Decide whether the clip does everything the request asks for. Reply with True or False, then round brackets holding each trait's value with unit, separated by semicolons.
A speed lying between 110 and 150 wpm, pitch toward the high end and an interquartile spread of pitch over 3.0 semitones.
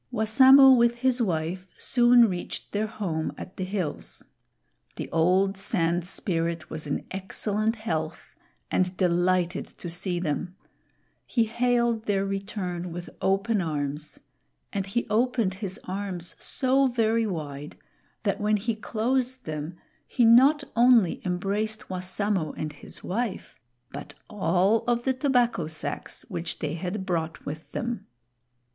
True (135 wpm; 195 Hz; 4.9 semitones)